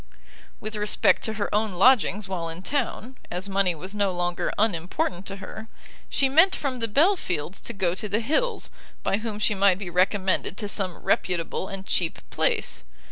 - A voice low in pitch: No, high, 200 Hz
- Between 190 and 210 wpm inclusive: No, average, 180 wpm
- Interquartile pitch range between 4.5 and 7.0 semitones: No, average, 3.3 semitones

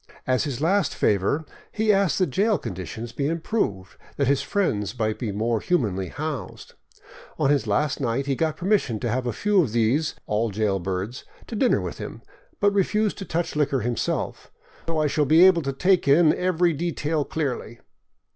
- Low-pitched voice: No, medium, 145 Hz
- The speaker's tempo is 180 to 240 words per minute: Yes, average, 195 wpm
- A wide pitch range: Yes, wide, 7.0 semitones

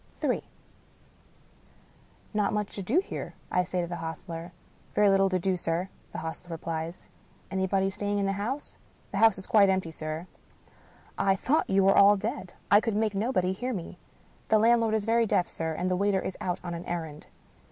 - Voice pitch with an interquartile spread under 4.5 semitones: Yes, average, 3.1 semitones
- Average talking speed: No, fast, 215 wpm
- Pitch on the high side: Yes, high, 195 Hz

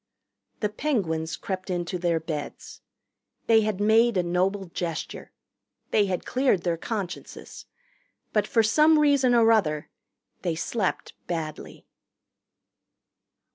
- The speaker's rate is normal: No, slow, 115 wpm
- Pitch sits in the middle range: No, high, 195 Hz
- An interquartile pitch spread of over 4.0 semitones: Yes, average, 4.7 semitones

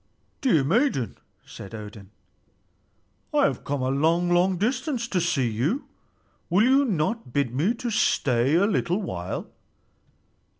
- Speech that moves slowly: Yes, slow, 130 wpm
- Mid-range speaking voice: Yes, medium, 170 Hz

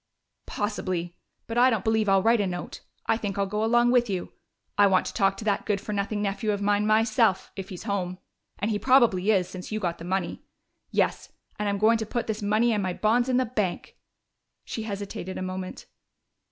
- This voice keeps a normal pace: No, fast, 215 wpm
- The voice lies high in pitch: Yes, high, 205 Hz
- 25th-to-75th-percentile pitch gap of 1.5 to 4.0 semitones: Yes, narrow, 2.6 semitones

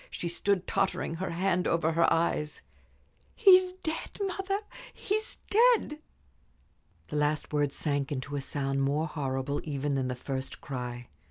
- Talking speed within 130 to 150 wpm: Yes, average, 145 wpm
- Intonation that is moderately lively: No, wide, 6.4 semitones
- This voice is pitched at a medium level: Yes, medium, 155 Hz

